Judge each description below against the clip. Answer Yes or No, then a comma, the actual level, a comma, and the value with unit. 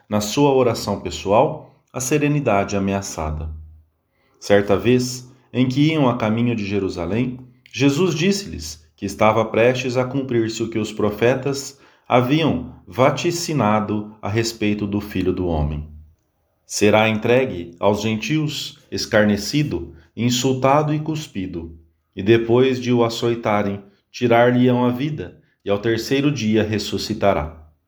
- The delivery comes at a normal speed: No, slow, 120 wpm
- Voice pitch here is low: Yes, low, 110 Hz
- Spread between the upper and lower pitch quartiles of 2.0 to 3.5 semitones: No, average, 4.6 semitones